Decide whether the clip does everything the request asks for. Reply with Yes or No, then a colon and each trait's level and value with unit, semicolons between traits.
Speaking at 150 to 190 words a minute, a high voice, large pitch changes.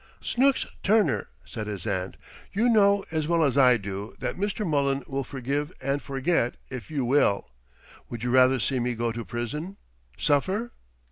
No: average, 165 wpm; low, 135 Hz; wide, 6.4 semitones